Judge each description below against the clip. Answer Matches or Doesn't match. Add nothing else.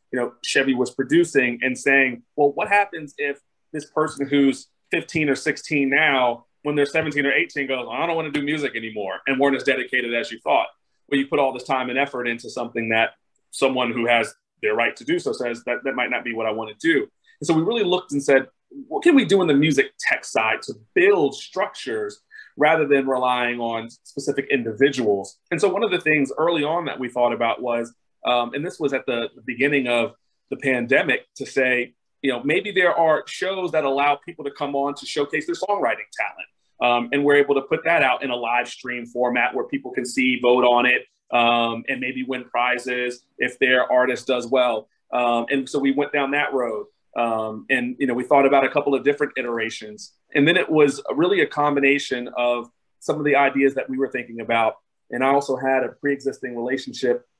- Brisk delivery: Matches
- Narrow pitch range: Doesn't match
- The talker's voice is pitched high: Doesn't match